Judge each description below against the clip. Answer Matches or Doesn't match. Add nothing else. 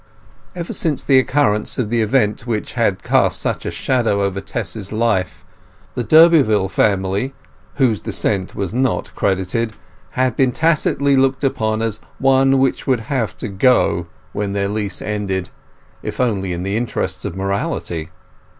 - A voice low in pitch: Matches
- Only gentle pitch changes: Doesn't match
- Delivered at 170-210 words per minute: Doesn't match